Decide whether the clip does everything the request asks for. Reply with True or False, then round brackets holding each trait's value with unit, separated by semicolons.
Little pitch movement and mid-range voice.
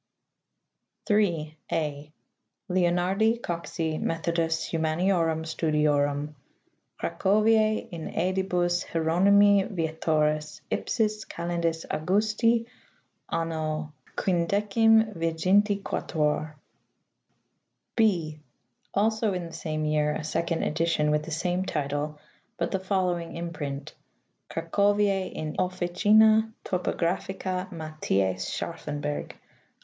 False (4.0 semitones; 170 Hz)